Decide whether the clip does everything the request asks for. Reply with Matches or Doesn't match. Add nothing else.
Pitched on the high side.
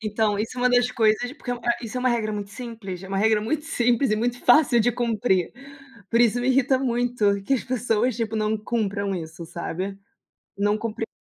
Matches